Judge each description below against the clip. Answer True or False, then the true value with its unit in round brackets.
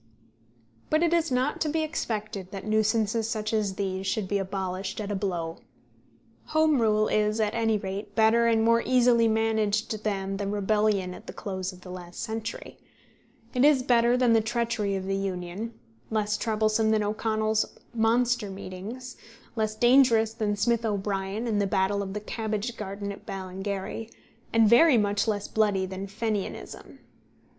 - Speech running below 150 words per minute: False (165 wpm)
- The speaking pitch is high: True (215 Hz)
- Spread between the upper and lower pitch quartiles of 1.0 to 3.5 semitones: True (2.6 semitones)